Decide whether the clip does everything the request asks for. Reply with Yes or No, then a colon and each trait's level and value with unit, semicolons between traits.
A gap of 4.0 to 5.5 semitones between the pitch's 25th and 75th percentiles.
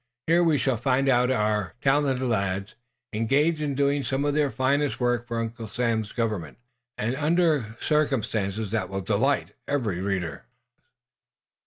Yes: average, 4.9 semitones